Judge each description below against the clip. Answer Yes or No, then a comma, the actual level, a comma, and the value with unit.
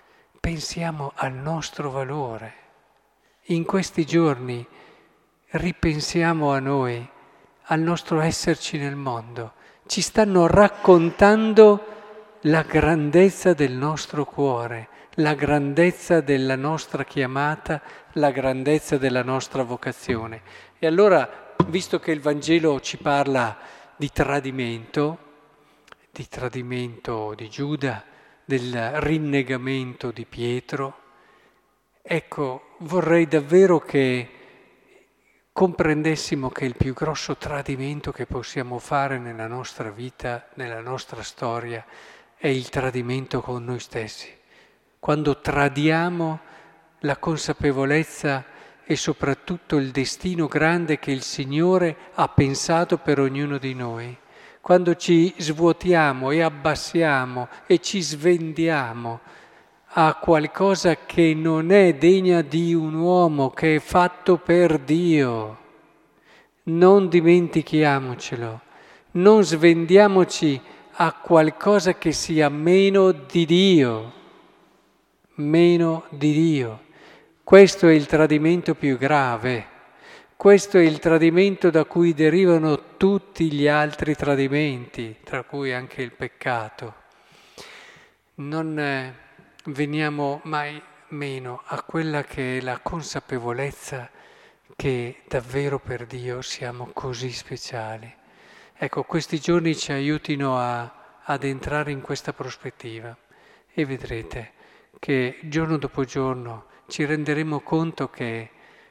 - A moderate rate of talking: No, slow, 105 wpm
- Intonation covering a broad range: No, average, 4.0 semitones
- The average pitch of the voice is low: No, medium, 150 Hz